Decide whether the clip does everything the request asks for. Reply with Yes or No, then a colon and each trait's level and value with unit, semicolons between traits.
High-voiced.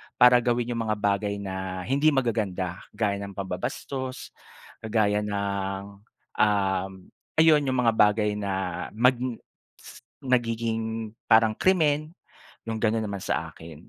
No: low, 110 Hz